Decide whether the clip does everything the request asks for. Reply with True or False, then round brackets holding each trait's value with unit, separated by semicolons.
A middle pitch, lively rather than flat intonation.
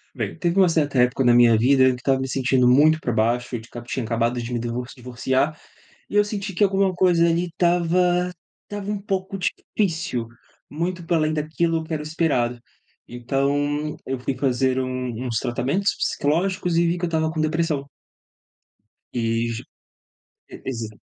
True (150 Hz; 5.7 semitones)